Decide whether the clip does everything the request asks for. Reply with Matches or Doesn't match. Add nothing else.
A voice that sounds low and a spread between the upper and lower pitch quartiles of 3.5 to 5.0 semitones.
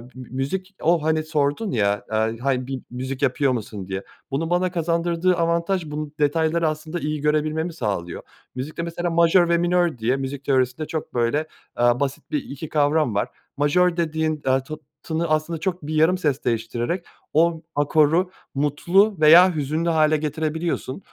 Doesn't match